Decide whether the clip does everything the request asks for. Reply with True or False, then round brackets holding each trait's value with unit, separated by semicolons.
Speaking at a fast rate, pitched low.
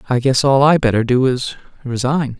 False (175 wpm; 130 Hz)